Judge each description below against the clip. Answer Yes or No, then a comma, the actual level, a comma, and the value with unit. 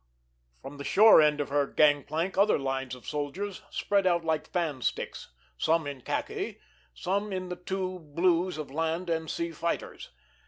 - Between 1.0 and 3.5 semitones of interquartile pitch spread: No, average, 4.1 semitones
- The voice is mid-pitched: Yes, medium, 165 Hz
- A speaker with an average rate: Yes, average, 170 wpm